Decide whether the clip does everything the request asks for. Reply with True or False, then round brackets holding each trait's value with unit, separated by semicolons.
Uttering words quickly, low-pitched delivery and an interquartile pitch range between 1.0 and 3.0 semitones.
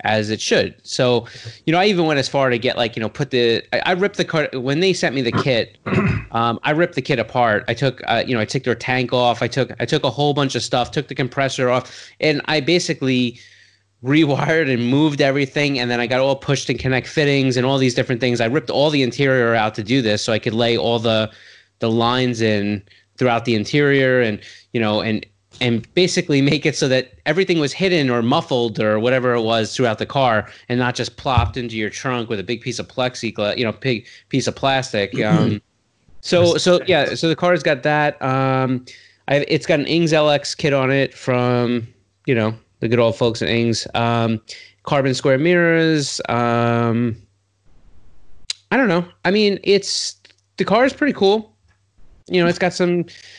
False (215 wpm; 125 Hz; 4.1 semitones)